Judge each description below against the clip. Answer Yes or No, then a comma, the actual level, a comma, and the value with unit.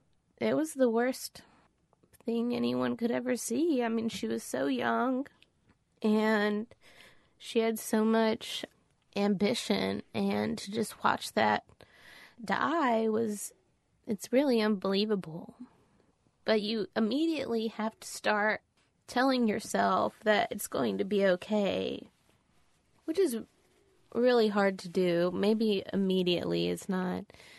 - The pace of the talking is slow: Yes, slow, 120 wpm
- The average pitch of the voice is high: Yes, high, 215 Hz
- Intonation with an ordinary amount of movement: Yes, average, 3.8 semitones